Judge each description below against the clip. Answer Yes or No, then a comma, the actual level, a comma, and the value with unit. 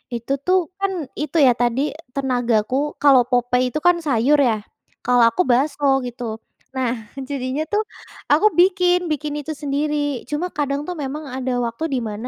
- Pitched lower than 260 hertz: No, very high, 275 Hz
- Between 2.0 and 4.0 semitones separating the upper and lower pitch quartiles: Yes, average, 3.6 semitones